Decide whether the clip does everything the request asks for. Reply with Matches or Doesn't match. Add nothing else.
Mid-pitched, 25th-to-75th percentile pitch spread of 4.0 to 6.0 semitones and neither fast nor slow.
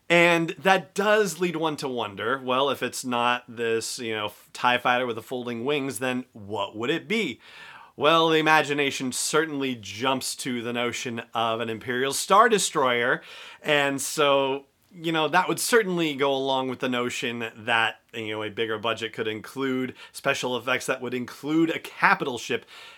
Doesn't match